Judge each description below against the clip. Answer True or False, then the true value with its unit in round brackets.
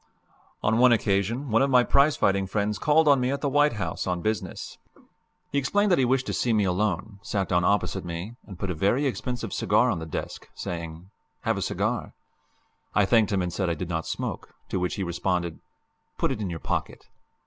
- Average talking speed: False (215 wpm)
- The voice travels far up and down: True (5.9 semitones)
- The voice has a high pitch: False (100 Hz)